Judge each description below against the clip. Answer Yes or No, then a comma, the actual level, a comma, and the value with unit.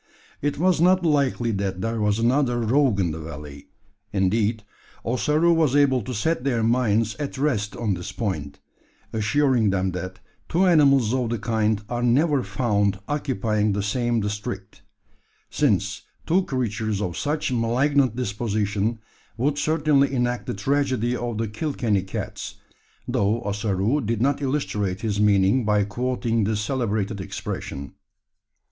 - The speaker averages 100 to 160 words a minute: Yes, average, 140 wpm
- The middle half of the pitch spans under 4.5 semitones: No, average, 4.8 semitones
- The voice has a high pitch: No, low, 115 Hz